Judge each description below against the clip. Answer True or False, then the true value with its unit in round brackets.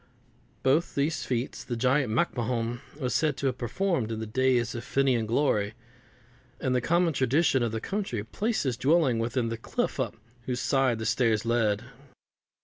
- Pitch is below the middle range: True (125 Hz)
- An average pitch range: True (3.1 semitones)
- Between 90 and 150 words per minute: False (170 wpm)